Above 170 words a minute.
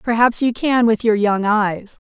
Yes: fast, 205 wpm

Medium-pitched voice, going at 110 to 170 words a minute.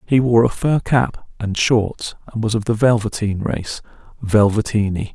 No: low, 110 Hz; average, 165 wpm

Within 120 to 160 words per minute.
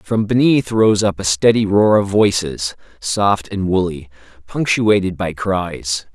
Yes: average, 145 wpm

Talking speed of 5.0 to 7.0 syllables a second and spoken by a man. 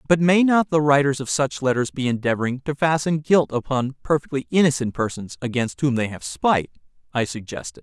Yes: 5.7 syllables/s; male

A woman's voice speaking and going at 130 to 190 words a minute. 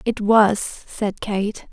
Yes: female; average, 140 wpm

